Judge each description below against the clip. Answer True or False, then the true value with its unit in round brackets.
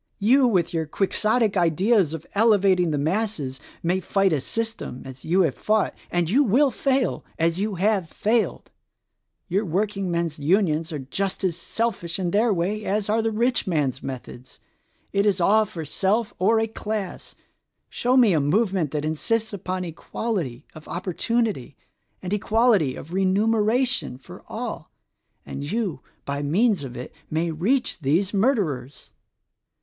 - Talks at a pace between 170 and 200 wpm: False (155 wpm)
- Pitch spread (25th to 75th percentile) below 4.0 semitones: False (5.2 semitones)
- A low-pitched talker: False (190 Hz)